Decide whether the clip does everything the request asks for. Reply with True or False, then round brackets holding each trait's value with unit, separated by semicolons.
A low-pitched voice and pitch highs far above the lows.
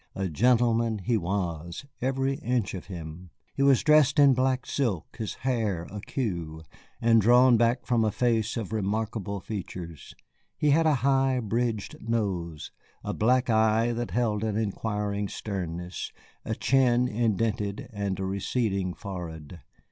False (110 Hz; 4.2 semitones)